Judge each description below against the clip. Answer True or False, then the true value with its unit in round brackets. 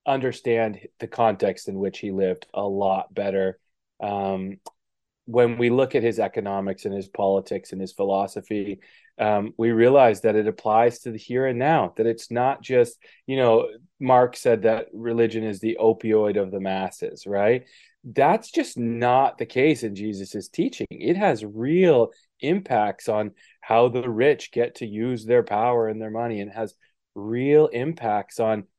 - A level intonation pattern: False (3.3 semitones)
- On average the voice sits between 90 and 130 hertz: True (115 Hz)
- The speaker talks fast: False (165 wpm)